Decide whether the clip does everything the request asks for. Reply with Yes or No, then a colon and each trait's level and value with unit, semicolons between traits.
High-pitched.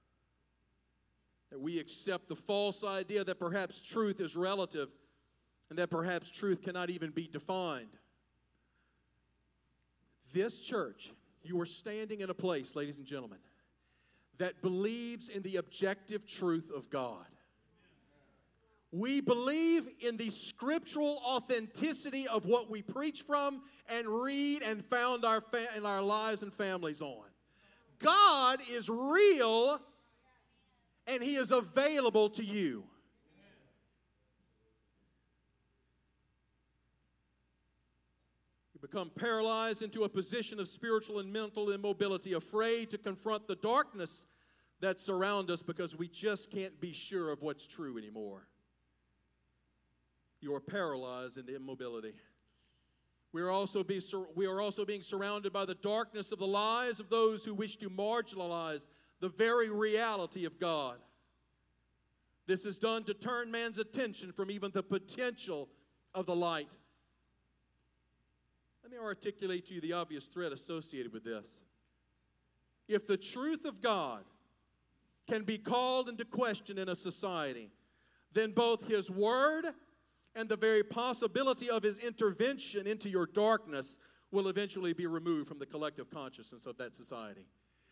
Yes: high, 195 Hz